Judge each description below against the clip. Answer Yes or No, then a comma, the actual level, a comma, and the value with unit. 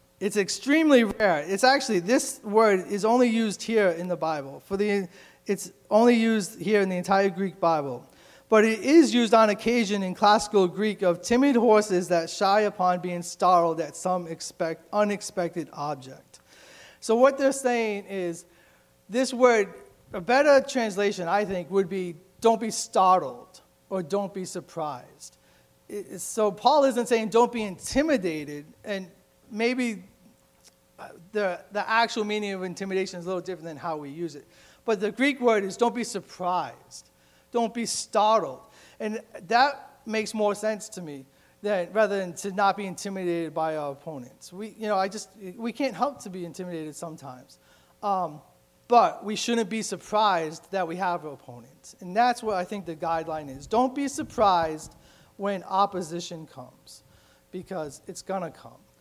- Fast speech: No, average, 165 wpm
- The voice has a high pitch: Yes, high, 195 Hz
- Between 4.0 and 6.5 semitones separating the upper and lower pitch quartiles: Yes, average, 4.3 semitones